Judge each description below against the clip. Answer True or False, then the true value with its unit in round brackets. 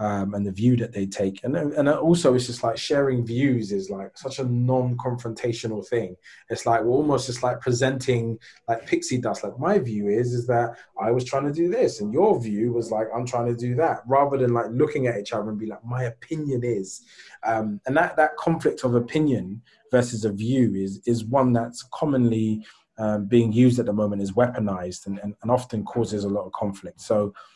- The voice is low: True (120 Hz)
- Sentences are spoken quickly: True (215 wpm)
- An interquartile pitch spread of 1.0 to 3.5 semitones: True (3.1 semitones)